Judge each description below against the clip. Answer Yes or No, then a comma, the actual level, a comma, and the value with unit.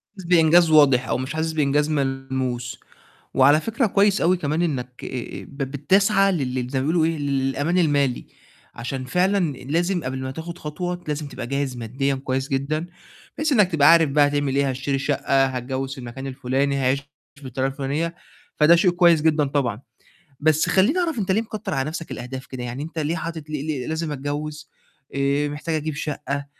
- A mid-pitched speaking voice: Yes, medium, 145 Hz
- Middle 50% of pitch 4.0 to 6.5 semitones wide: No, average, 3.6 semitones